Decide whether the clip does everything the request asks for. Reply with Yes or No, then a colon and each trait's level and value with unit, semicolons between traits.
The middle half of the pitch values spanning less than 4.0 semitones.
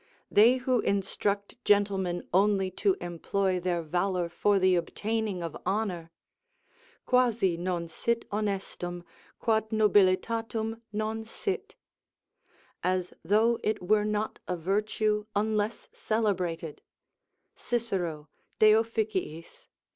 Yes: average, 3.3 semitones